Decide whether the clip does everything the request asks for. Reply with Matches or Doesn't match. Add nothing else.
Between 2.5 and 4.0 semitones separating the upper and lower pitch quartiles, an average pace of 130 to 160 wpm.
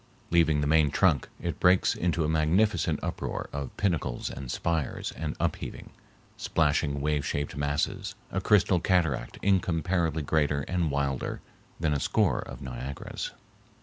Matches